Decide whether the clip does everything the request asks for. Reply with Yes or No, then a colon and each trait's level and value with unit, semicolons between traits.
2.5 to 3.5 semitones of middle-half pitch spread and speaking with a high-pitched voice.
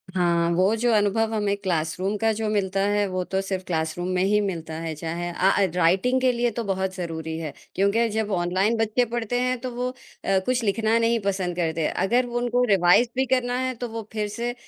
No: average, 4.5 semitones; high, 200 Hz